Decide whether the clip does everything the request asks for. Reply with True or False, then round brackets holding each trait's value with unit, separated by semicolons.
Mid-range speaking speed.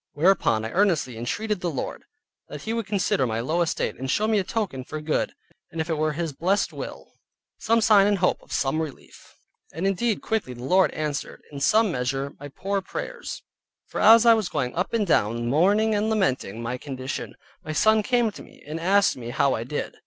False (210 wpm)